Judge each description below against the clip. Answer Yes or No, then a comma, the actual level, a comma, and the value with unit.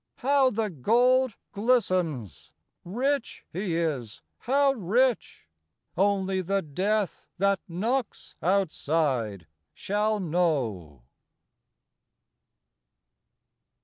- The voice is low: No, high, 195 Hz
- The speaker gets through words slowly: Yes, slow, 75 wpm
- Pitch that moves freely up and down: Yes, wide, 6.2 semitones